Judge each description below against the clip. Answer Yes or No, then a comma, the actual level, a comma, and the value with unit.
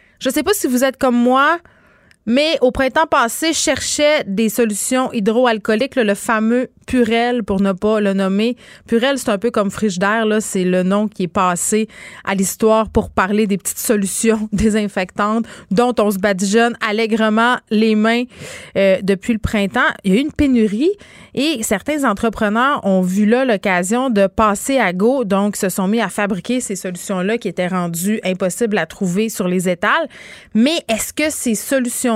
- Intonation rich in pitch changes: No, average, 3.6 semitones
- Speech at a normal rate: Yes, average, 180 wpm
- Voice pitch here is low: No, high, 220 Hz